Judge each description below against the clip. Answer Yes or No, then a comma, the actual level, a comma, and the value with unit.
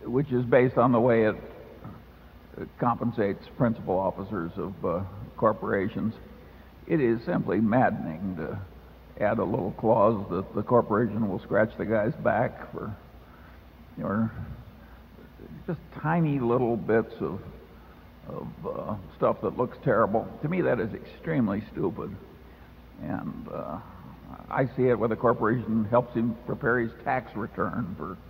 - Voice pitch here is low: Yes, low, 115 Hz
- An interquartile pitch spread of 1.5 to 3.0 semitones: No, average, 3.5 semitones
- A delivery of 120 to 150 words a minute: Yes, average, 140 wpm